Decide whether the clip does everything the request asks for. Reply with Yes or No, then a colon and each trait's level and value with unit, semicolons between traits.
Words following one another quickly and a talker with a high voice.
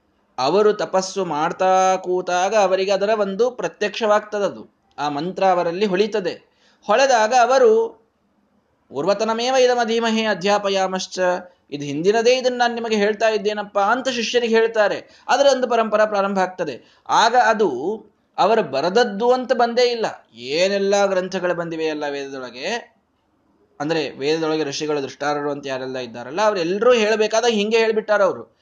Yes: fast, 120 wpm; high, 205 Hz